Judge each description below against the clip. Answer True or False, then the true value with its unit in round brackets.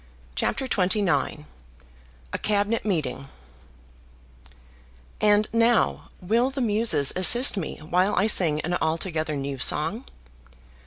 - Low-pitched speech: False (190 Hz)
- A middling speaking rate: False (105 wpm)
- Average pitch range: False (5.9 semitones)